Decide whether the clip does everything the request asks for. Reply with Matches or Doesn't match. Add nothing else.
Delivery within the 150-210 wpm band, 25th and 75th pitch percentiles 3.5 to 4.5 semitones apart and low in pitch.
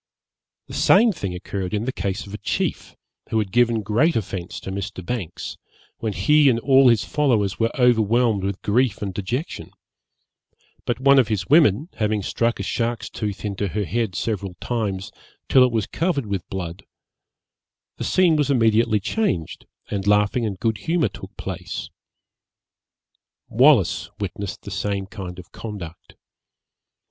Matches